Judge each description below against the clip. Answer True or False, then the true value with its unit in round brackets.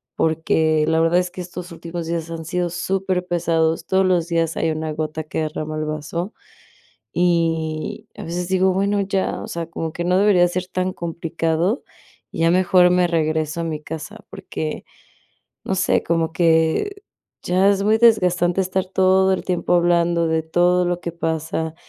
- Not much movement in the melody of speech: True (2.2 semitones)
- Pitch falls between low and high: True (170 Hz)